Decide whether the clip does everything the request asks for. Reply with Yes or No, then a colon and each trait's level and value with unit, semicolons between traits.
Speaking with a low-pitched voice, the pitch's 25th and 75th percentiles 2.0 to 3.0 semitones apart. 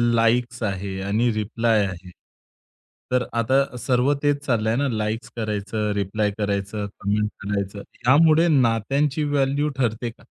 No: low, 115 Hz; average, 4.0 semitones